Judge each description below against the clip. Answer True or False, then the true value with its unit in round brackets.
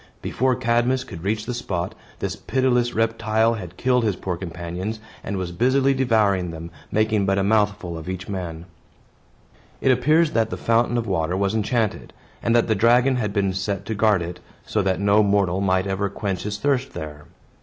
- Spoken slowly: False (185 wpm)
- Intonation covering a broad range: False (4.0 semitones)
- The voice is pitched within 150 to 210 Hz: False (105 Hz)